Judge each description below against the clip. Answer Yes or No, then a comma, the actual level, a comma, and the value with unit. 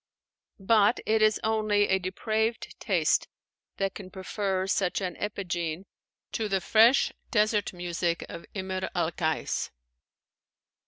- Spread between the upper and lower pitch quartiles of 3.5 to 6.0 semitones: No, average, 2.9 semitones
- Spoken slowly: Yes, slow, 120 wpm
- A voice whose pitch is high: Yes, high, 195 Hz